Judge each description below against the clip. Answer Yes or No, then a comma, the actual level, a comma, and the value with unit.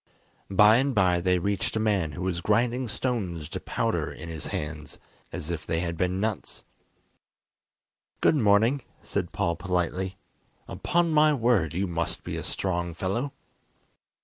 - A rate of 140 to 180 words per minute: Yes, average, 150 wpm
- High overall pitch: No, very low, 95 Hz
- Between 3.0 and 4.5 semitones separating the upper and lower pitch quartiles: No, average, 5.0 semitones